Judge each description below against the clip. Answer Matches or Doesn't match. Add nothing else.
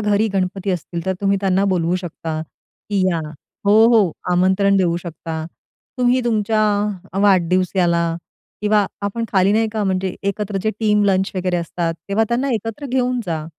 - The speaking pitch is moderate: Doesn't match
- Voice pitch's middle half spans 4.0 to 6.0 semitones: Doesn't match